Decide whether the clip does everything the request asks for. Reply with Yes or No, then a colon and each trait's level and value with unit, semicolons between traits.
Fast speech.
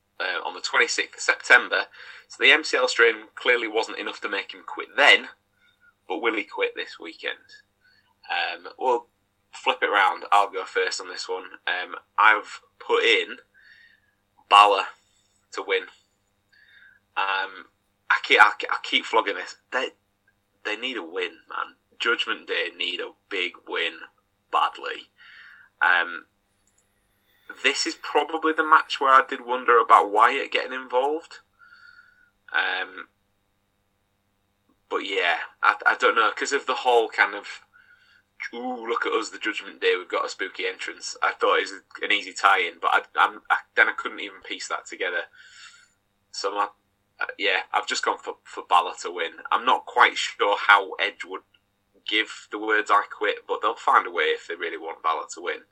No: average, 165 wpm